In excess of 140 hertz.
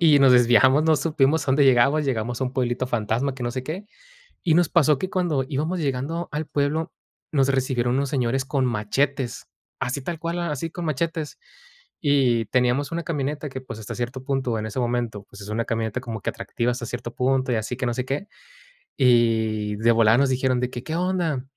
No: low, 130 Hz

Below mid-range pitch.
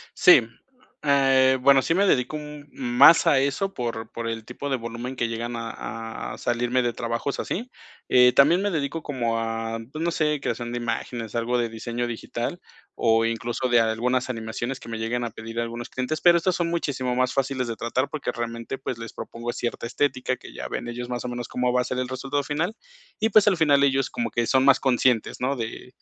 Yes: low, 125 Hz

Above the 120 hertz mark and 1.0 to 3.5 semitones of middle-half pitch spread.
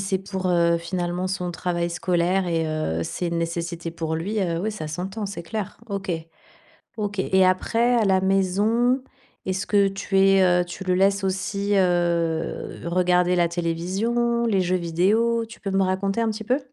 Yes: medium, 185 Hz; average, 2.7 semitones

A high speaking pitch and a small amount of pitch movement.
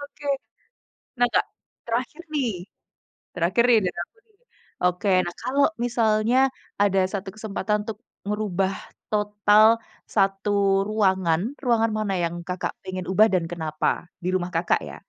No: high, 205 Hz; average, 3.3 semitones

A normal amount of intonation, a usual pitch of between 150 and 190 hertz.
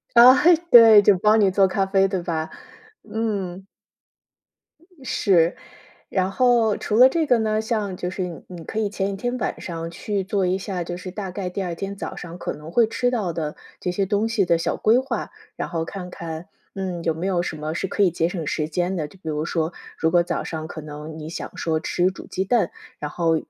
Yes: average, 3.7 semitones; medium, 185 Hz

